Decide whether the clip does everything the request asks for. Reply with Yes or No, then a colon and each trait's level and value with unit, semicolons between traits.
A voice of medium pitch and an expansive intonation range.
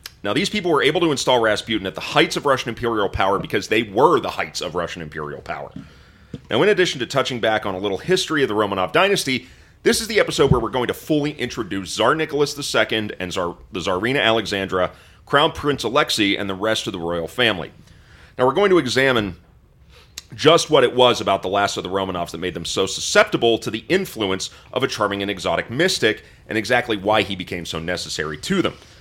No: low, 110 Hz; wide, 6.1 semitones